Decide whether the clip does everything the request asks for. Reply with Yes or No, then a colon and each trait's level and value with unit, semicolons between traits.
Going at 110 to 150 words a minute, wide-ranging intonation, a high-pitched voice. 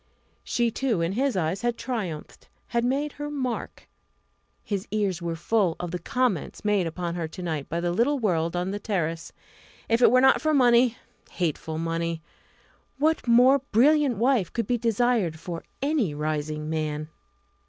No: average, 165 wpm; wide, 6.7 semitones; high, 200 Hz